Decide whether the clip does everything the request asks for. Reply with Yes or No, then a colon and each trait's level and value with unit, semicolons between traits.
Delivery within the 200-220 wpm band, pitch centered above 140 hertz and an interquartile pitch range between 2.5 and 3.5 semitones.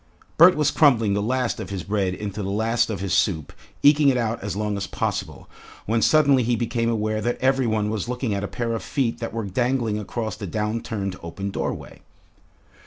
No: fast, 205 wpm; low, 110 Hz; average, 3.2 semitones